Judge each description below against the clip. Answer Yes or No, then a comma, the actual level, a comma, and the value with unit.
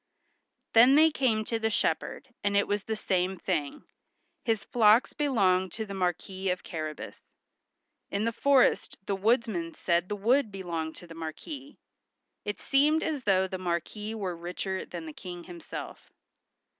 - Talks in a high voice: Yes, high, 200 Hz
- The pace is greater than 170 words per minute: No, average, 155 wpm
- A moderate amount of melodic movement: Yes, average, 4.3 semitones